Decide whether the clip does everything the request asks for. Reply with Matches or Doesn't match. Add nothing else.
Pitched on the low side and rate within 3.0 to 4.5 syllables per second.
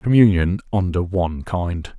Matches